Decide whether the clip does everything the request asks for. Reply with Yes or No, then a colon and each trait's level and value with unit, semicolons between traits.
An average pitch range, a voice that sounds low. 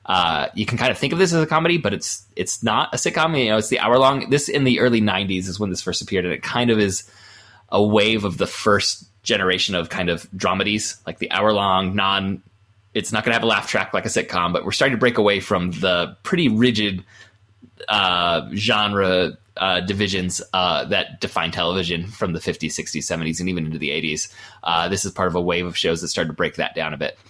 Yes: average, 3.2 semitones; low, 100 Hz